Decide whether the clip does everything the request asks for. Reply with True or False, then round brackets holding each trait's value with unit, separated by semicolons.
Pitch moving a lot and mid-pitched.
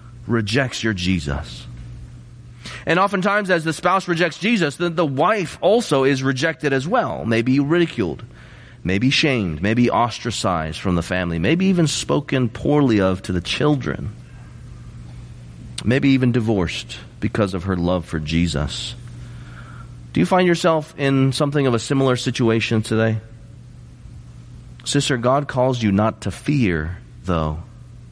False (6.1 semitones; 120 Hz)